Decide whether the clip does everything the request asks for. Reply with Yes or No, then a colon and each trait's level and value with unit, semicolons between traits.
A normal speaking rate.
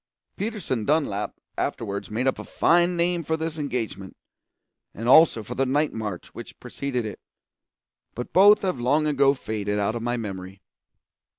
Yes: average, 160 wpm